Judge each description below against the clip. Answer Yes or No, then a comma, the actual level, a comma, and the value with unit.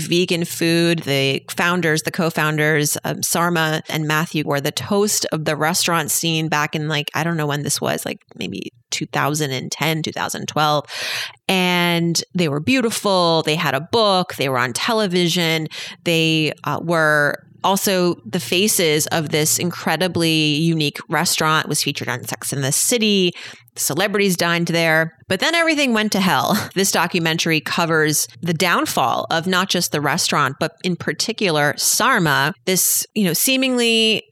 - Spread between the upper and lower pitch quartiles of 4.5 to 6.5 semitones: No, average, 3.1 semitones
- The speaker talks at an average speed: Yes, average, 155 wpm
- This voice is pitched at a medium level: Yes, medium, 165 Hz